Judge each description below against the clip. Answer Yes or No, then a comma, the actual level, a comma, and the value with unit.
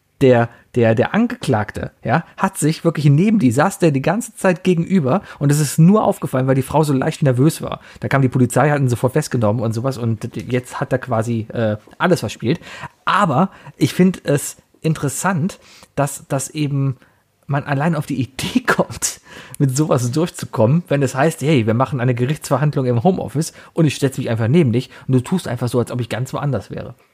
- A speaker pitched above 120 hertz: Yes, medium, 140 Hz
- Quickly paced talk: Yes, fast, 200 wpm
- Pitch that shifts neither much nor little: Yes, average, 4.4 semitones